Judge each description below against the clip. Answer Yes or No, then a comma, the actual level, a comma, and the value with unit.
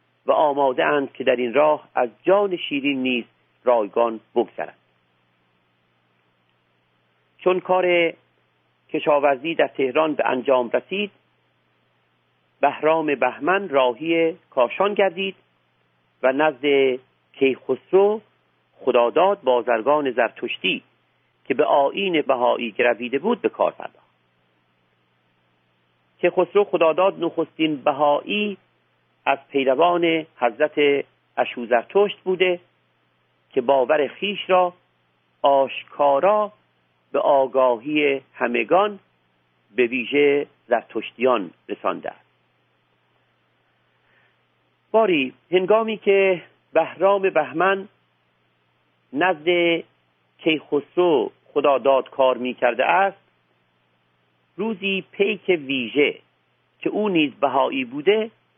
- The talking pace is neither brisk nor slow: No, slow, 85 wpm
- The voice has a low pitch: Yes, low, 130 Hz